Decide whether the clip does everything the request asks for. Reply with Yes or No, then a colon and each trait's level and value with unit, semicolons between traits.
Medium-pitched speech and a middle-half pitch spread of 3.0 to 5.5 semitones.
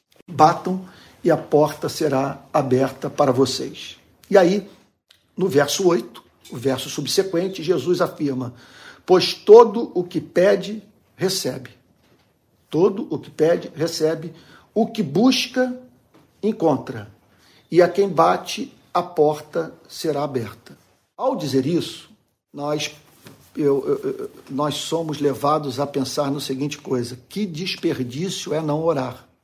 Yes: medium, 155 Hz; average, 5.2 semitones